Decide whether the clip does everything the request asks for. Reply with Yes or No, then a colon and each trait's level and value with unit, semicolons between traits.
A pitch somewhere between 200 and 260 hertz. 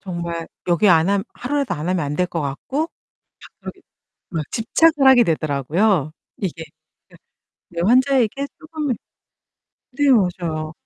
No: medium, 185 Hz